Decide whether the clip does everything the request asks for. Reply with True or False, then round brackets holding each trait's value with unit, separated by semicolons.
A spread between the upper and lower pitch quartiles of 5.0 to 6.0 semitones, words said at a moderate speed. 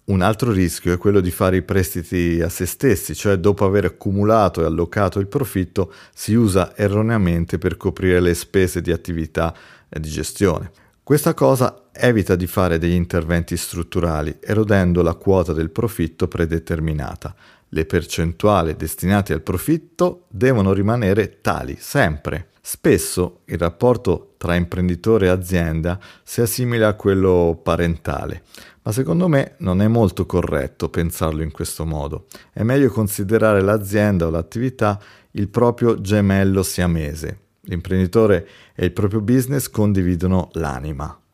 False (3.7 semitones; 140 wpm)